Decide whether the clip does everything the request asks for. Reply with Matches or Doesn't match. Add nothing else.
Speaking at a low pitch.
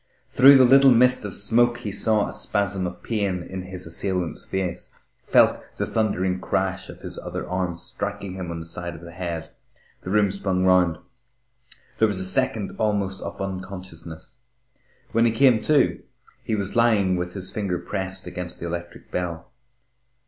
Matches